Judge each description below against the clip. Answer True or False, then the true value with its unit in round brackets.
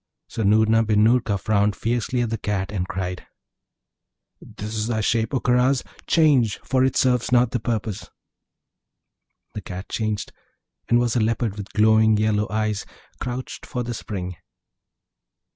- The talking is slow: False (150 wpm)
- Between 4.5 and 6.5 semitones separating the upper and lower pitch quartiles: False (2.5 semitones)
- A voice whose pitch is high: False (110 Hz)